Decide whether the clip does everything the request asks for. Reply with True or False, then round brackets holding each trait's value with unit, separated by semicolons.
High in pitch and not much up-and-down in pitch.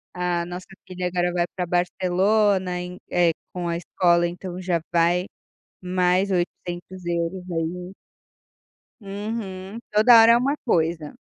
False (180 Hz; 1.5 semitones)